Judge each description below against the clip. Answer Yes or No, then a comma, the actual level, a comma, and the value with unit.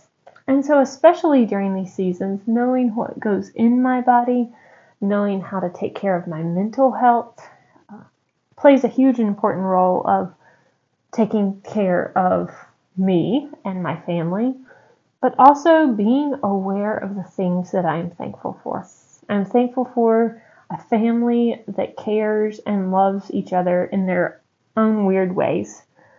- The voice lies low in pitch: No, high, 215 Hz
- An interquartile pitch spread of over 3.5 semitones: Yes, average, 4.5 semitones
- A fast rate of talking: No, average, 140 wpm